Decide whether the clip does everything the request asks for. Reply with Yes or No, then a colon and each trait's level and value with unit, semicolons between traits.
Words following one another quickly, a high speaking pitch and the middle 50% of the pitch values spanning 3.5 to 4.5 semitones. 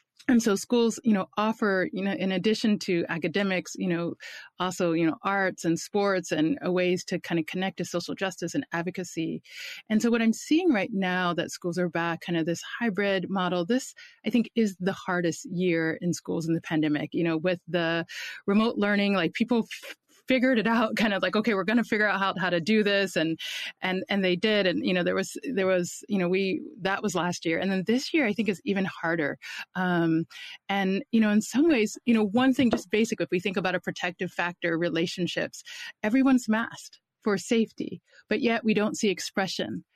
Yes: fast, 215 wpm; high, 195 Hz; average, 3.9 semitones